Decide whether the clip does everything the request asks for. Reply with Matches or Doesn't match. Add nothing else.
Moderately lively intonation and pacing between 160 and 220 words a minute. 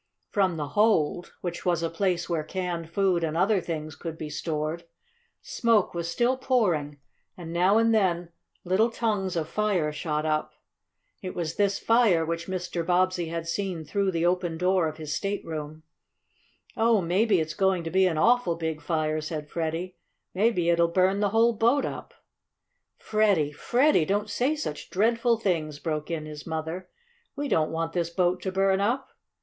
Matches